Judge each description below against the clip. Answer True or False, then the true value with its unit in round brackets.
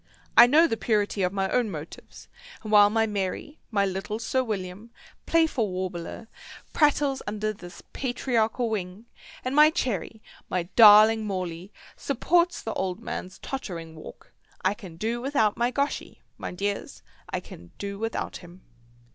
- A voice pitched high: True (215 Hz)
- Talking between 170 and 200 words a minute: False (150 wpm)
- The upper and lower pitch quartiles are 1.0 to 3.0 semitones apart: False (4.4 semitones)